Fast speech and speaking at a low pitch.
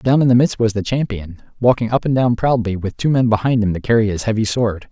Yes: fast, 270 wpm; low, 115 Hz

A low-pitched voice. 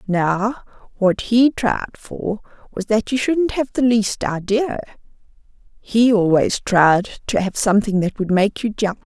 No: high, 215 Hz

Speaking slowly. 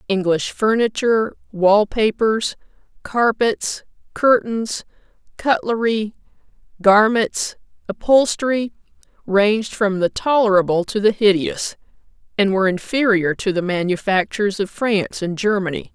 Yes: slow, 100 wpm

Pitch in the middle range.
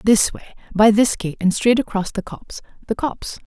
No: high, 215 Hz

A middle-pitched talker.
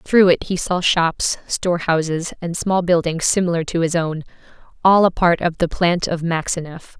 Yes: medium, 170 Hz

